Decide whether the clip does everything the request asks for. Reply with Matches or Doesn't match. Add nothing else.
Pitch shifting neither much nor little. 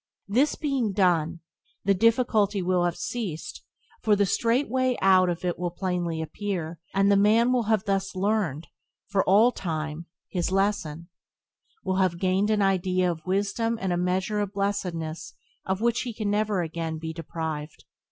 Matches